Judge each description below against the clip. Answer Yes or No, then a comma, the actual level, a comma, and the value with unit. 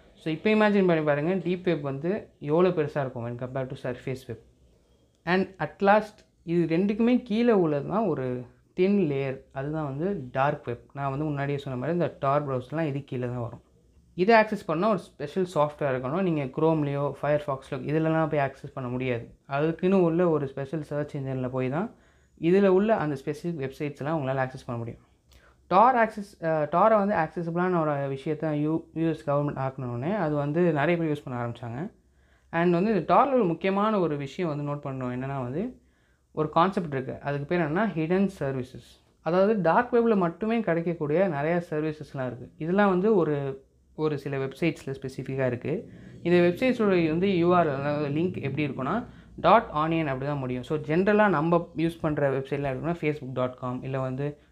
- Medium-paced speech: No, fast, 165 wpm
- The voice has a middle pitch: Yes, medium, 150 Hz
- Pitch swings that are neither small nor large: Yes, average, 4.7 semitones